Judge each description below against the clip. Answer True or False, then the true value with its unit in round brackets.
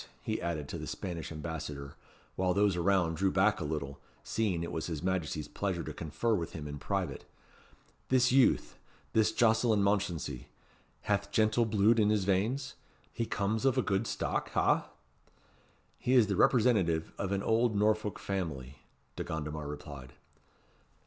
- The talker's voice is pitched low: True (95 Hz)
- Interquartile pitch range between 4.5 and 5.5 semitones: True (5.2 semitones)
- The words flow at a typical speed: True (155 wpm)